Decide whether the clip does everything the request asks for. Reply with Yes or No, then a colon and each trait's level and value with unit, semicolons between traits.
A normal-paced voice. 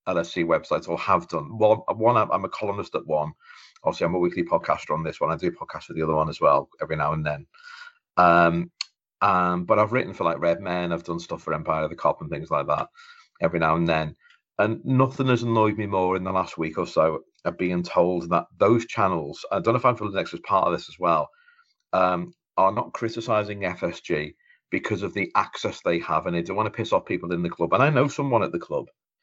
No: fast, 240 wpm